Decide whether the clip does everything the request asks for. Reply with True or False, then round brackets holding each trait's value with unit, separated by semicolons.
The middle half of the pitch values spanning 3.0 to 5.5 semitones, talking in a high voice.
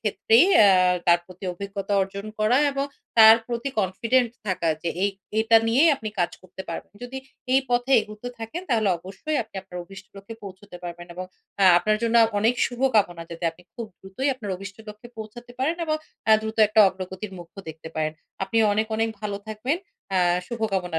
True (3.6 semitones; 210 Hz)